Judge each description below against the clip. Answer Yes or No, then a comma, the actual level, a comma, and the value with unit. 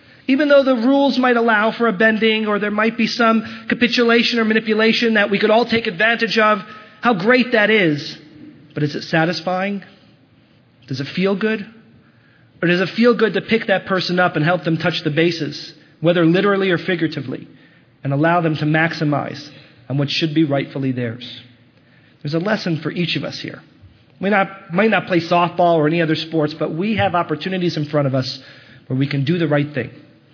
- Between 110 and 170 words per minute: No, average, 195 wpm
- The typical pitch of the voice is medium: Yes, medium, 175 Hz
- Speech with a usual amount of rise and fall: No, wide, 6.5 semitones